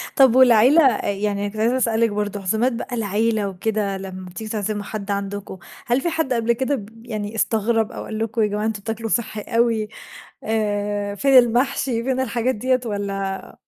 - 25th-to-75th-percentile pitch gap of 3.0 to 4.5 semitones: No, narrow, 2.6 semitones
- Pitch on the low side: No, high, 220 Hz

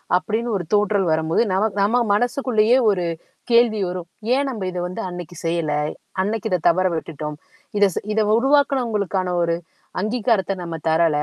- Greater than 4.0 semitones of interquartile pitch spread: Yes, average, 4.6 semitones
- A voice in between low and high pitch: No, high, 200 Hz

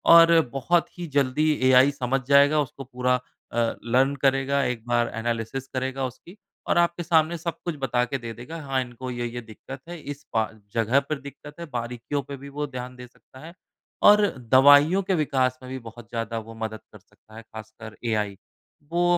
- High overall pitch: No, low, 130 Hz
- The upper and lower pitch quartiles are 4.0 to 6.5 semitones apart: No, average, 3.4 semitones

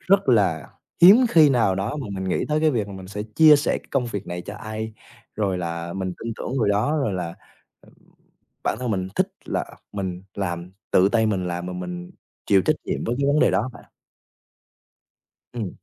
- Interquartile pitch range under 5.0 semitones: No, average, 5.3 semitones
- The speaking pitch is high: No, low, 100 Hz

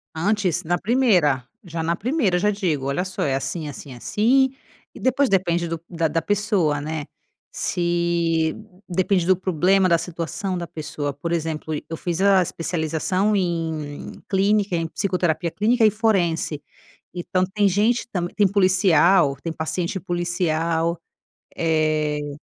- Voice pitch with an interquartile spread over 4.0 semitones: No, average, 3.3 semitones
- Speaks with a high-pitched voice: No, medium, 175 Hz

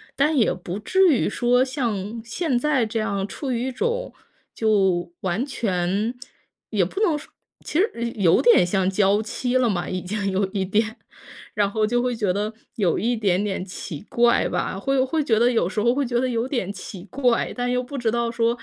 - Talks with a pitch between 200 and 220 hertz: No, high, 230 Hz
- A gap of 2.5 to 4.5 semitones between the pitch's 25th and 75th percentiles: Yes, average, 4.2 semitones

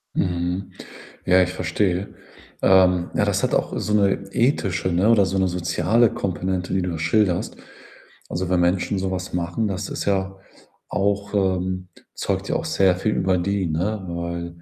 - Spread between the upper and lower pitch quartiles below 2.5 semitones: Yes, narrow, 1.9 semitones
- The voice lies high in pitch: No, very low, 95 Hz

